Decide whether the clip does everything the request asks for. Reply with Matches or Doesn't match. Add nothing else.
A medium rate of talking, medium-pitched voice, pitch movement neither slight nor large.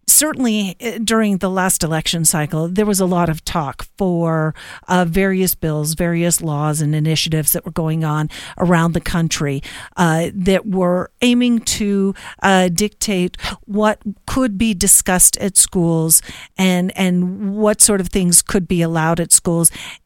Matches